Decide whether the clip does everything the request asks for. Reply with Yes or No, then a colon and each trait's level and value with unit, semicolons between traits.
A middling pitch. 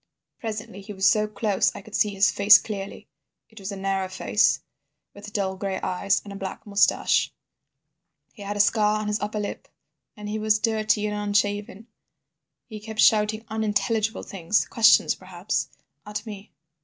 No: high, 210 Hz